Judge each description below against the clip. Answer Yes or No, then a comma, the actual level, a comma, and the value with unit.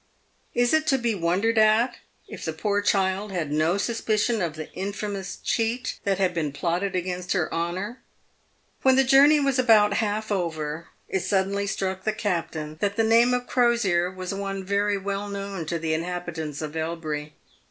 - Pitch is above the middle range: Yes, high, 195 Hz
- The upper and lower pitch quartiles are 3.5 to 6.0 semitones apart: Yes, average, 4.1 semitones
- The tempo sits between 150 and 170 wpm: No, average, 180 wpm